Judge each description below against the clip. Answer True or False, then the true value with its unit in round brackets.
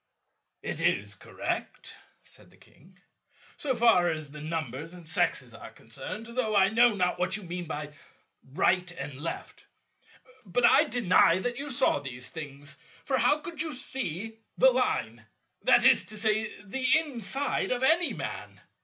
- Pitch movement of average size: False (7.2 semitones)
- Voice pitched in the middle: False (210 Hz)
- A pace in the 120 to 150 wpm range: False (160 wpm)